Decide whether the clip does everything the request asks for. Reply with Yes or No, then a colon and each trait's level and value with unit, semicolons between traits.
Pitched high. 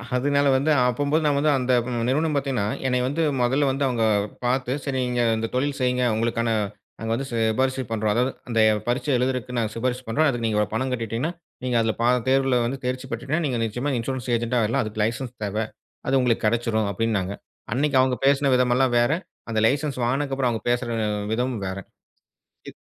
No: low, 125 Hz